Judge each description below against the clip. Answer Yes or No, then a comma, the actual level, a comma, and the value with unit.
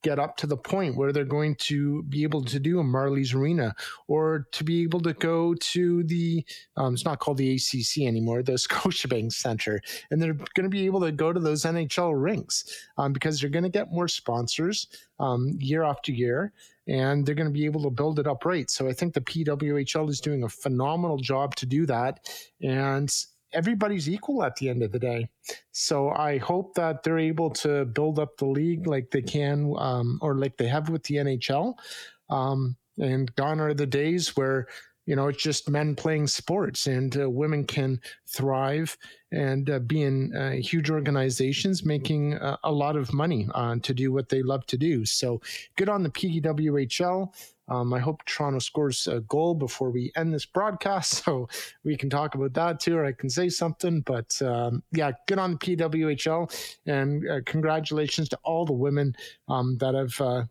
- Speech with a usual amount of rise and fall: Yes, average, 3.4 semitones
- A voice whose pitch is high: No, medium, 145 Hz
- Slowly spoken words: No, average, 200 wpm